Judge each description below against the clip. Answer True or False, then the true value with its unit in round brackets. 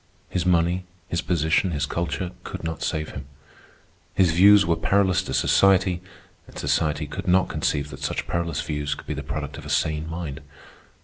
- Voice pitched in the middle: False (85 Hz)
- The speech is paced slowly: False (180 wpm)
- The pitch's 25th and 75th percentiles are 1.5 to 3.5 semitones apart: True (3.1 semitones)